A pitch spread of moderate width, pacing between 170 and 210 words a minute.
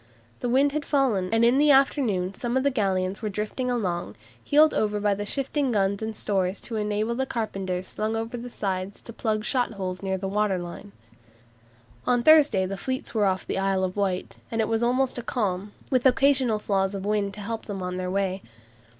Yes: average, 4.1 semitones; average, 200 wpm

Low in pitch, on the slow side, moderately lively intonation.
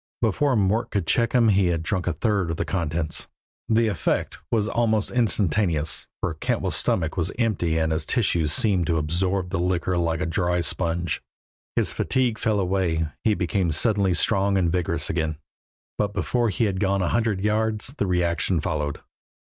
No: very low, 95 Hz; average, 175 wpm; average, 4.3 semitones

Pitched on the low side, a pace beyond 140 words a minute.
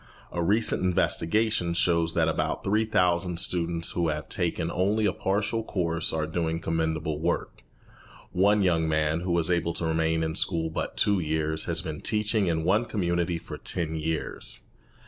Yes: very low, 85 Hz; average, 165 wpm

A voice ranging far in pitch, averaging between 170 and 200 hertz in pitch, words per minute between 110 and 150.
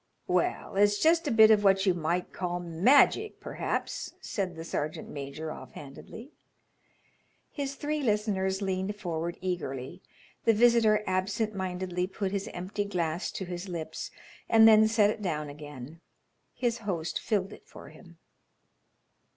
No: average, 3.9 semitones; high, 190 Hz; average, 145 wpm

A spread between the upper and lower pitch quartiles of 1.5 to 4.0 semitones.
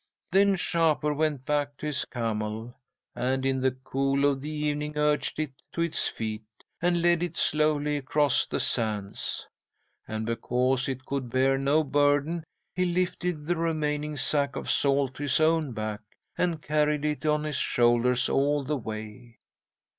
Yes: average, 3.0 semitones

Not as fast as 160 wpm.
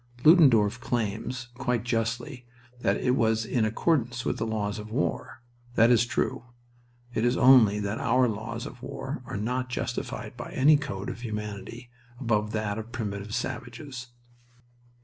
Yes: average, 150 wpm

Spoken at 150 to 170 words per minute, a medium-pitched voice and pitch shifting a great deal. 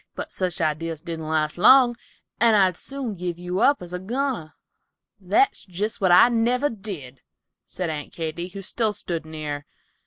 Yes: average, 165 wpm; medium, 180 Hz; wide, 5.8 semitones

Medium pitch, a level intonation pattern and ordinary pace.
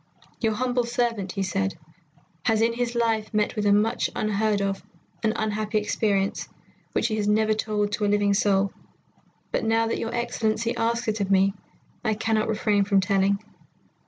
No: high, 215 Hz; narrow, 2.0 semitones; average, 170 wpm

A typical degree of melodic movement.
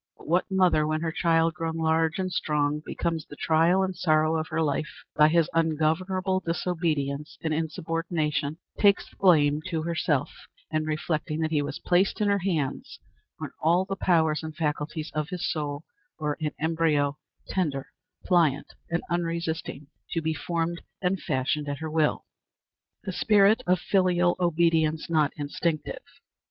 No: narrow, 2.3 semitones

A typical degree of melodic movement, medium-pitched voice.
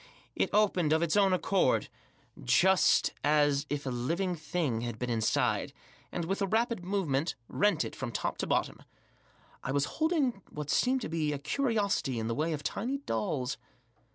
No: wide, 6.3 semitones; medium, 165 Hz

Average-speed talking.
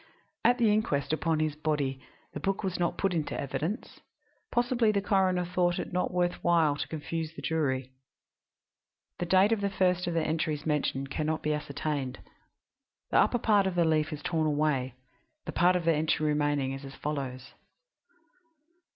Yes: average, 175 wpm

